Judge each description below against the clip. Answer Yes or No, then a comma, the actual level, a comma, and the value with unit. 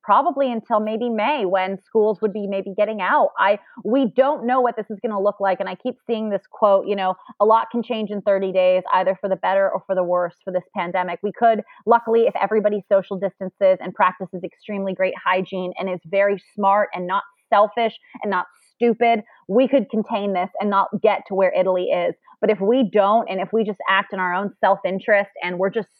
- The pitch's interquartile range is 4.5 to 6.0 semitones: No, average, 2.9 semitones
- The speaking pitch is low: No, high, 200 Hz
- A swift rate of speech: Yes, fast, 225 wpm